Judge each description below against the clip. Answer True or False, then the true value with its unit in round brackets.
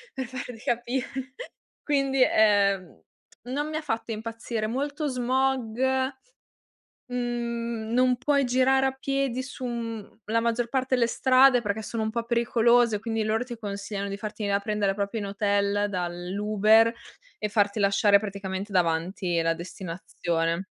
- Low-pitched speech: False (225 Hz)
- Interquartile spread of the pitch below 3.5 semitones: False (3.8 semitones)